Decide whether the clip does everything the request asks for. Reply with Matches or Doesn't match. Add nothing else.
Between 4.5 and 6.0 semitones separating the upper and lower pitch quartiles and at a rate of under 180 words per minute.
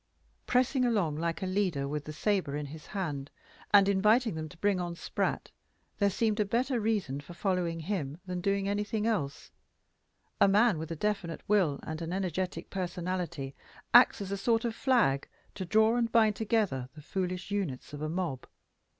Doesn't match